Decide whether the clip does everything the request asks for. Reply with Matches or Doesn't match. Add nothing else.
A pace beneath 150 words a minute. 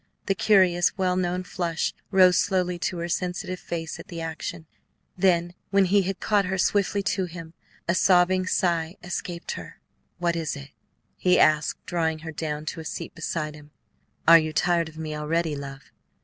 Doesn't match